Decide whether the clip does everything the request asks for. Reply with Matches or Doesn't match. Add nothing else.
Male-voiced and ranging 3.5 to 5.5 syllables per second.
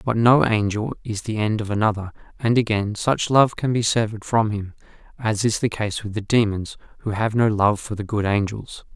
Matches